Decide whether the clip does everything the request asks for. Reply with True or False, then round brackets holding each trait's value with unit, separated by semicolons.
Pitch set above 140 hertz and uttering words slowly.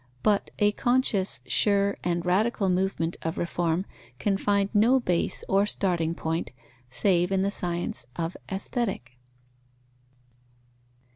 True (190 Hz; 120 wpm)